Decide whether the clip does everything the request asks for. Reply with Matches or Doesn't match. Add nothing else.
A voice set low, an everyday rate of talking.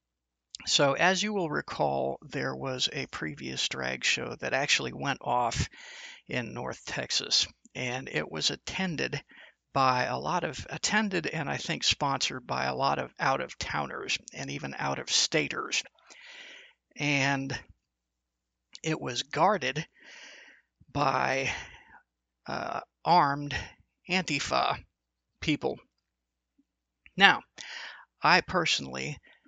Doesn't match